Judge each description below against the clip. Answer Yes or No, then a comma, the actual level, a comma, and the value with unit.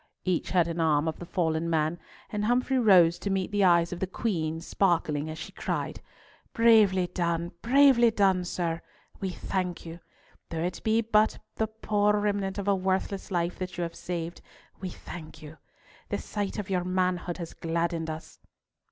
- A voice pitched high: No, medium, 180 Hz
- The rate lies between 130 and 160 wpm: No, average, 175 wpm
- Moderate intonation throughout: Yes, average, 3.5 semitones